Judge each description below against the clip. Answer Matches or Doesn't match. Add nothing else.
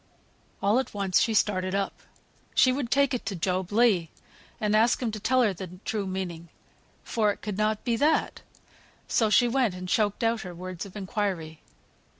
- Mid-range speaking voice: Doesn't match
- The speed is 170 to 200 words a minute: Matches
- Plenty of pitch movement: Doesn't match